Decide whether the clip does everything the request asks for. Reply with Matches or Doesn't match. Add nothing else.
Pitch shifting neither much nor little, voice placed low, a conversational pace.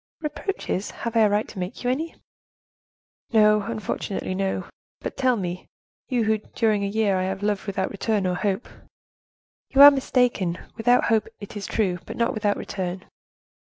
Doesn't match